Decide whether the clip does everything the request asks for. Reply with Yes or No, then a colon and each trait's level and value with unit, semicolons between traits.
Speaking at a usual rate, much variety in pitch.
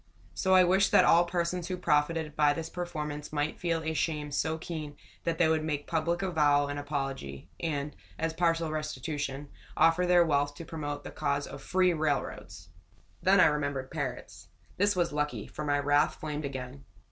No: average, 180 wpm; average, 2.7 semitones